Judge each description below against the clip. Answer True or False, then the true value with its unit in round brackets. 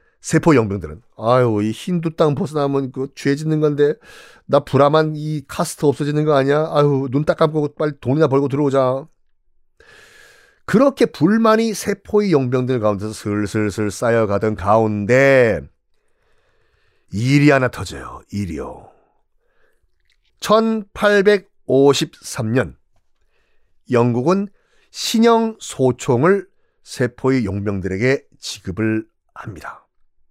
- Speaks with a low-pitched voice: False (145 Hz)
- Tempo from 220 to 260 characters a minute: True (230 characters per minute)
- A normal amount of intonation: False (7.7 semitones)